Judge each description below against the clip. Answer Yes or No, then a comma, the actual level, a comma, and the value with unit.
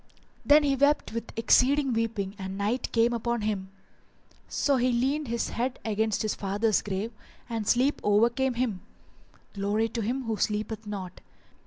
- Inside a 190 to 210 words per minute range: No, average, 155 wpm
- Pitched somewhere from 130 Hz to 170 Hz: No, high, 230 Hz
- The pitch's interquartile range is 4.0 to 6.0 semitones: No, average, 3.3 semitones